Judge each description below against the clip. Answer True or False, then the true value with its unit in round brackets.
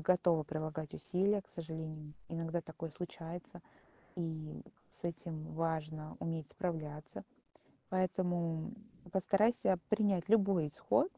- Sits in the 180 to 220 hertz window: False (165 Hz)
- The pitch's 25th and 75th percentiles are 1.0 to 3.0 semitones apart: True (2.7 semitones)